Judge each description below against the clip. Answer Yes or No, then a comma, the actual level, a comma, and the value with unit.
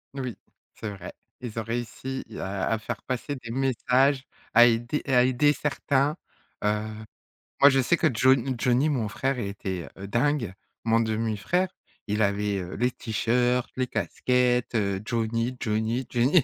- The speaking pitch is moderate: No, low, 120 Hz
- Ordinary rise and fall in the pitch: Yes, average, 3.3 semitones